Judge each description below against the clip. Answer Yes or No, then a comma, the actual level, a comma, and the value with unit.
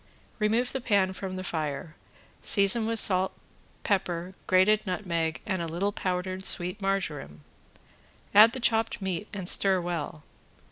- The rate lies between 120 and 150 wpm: Yes, average, 140 wpm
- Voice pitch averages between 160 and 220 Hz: Yes, high, 190 Hz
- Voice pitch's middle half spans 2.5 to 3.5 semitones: Yes, average, 3.0 semitones